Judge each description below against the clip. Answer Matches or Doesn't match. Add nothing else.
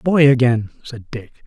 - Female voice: Doesn't match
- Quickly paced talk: Doesn't match